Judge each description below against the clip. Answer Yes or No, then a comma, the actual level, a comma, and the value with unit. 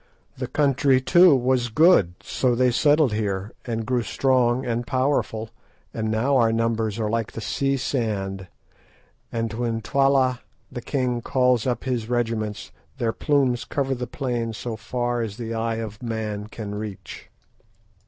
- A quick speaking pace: No, average, 155 wpm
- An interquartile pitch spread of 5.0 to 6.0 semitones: No, narrow, 2.6 semitones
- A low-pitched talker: Yes, low, 120 Hz